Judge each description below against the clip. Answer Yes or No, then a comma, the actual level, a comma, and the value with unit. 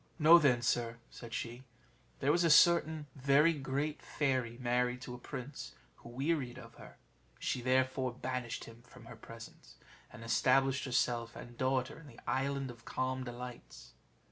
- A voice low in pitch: Yes, low, 130 Hz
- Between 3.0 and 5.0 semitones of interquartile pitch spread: No, narrow, 2.4 semitones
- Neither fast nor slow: Yes, average, 160 wpm